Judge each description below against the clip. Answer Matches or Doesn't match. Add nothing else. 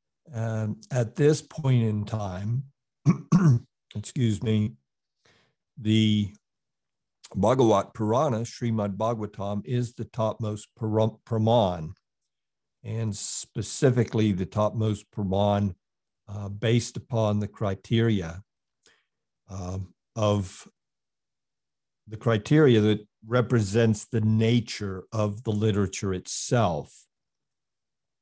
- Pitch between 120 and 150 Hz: Doesn't match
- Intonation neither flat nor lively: Doesn't match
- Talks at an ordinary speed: Doesn't match